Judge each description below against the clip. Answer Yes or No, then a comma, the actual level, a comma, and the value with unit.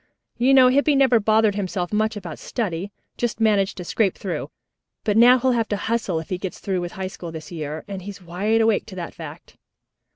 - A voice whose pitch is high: Yes, high, 205 Hz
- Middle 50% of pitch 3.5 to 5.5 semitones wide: Yes, average, 3.8 semitones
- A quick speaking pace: Yes, fast, 215 wpm